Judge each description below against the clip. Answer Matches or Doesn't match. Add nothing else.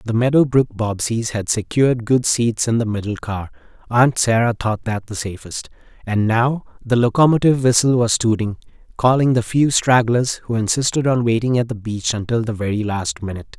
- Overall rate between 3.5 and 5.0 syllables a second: Doesn't match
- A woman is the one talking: Doesn't match